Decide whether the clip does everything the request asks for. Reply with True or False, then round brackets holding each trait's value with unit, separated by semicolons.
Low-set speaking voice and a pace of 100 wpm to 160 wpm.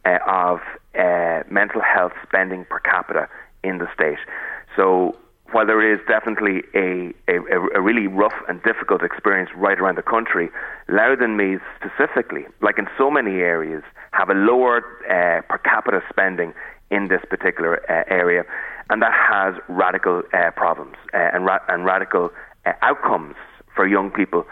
True (95 Hz; 155 wpm)